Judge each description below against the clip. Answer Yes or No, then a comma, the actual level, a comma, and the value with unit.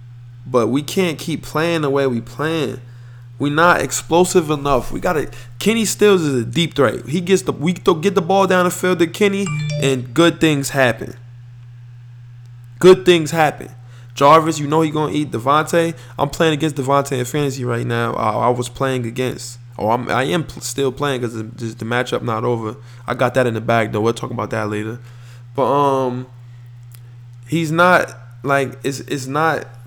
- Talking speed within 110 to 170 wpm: No, average, 185 wpm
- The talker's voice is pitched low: Yes, low, 130 Hz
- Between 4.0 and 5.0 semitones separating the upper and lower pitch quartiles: Yes, average, 4.7 semitones